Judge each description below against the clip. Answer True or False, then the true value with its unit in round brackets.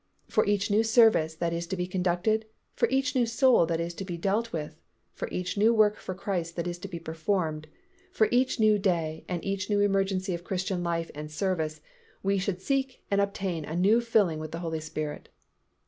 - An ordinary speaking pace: False (210 wpm)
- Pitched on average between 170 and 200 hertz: True (185 Hz)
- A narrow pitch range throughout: False (3.7 semitones)